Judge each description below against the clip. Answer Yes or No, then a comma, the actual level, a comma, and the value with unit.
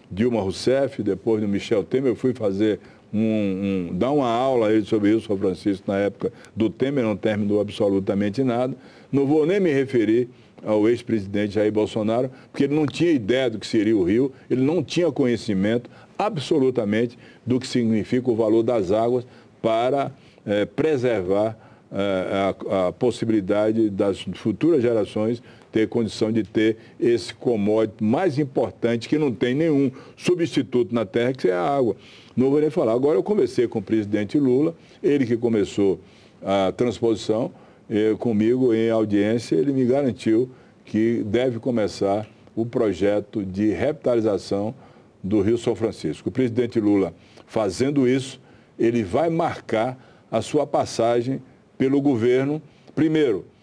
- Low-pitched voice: Yes, low, 115 Hz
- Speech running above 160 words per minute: No, average, 150 wpm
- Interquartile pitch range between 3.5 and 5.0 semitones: No, average, 3.1 semitones